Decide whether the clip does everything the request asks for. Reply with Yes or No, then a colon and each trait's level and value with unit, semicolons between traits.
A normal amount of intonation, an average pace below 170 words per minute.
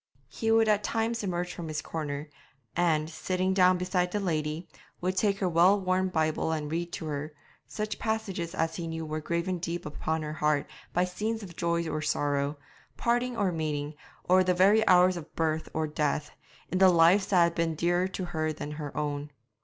No: average, 3.1 semitones; average, 195 wpm